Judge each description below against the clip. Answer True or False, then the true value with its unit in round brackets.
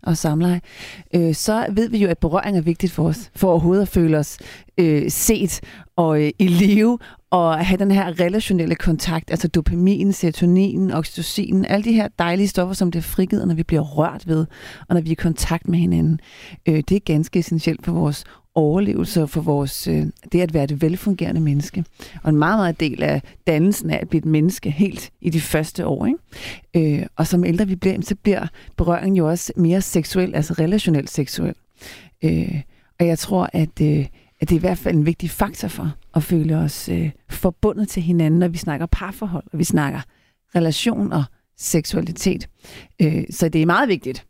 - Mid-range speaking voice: True (170 Hz)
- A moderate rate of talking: True (195 wpm)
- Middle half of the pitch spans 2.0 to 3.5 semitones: True (3.2 semitones)